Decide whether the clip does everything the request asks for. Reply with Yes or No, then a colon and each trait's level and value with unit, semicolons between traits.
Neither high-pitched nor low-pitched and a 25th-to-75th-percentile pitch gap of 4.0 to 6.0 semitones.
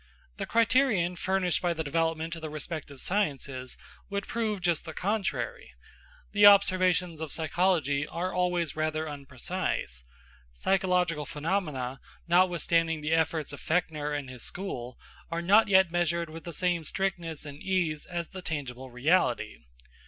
No: medium, 170 Hz; average, 3.6 semitones